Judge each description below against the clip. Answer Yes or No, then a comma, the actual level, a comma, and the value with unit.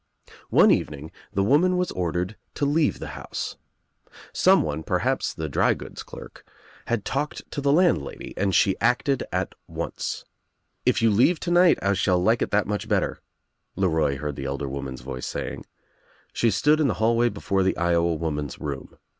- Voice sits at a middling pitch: No, very low, 95 Hz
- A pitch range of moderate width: No, wide, 8.3 semitones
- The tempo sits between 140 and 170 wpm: Yes, average, 165 wpm